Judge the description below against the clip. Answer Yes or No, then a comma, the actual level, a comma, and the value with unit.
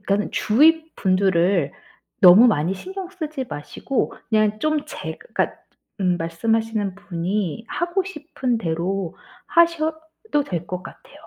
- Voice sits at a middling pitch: No, high, 215 Hz